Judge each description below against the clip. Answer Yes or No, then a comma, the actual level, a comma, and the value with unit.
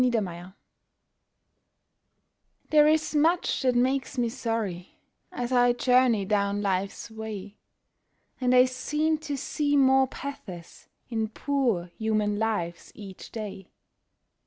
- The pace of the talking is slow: Yes, slow, 110 wpm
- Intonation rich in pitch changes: No, average, 4.6 semitones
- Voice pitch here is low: No, high, 235 Hz